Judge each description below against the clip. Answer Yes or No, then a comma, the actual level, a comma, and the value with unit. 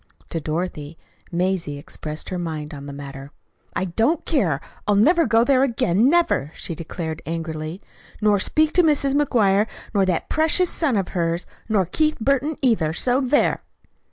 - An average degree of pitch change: No, wide, 8.9 semitones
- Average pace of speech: Yes, average, 160 wpm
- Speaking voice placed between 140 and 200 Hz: Yes, high, 190 Hz